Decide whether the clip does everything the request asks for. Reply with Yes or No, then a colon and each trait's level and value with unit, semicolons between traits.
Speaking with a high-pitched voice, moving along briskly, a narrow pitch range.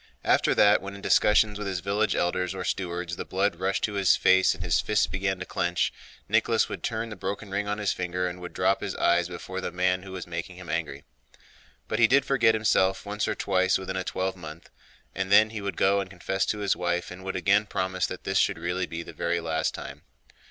No: very low, 95 Hz; fast, 230 wpm; narrow, 2.2 semitones